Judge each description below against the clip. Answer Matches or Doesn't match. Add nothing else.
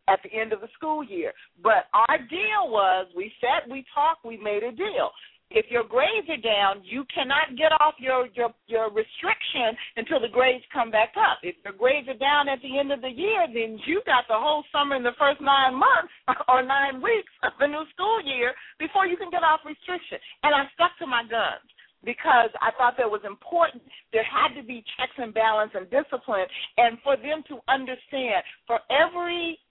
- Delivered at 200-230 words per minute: Matches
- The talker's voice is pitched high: Matches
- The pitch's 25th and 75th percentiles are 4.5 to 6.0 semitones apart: Matches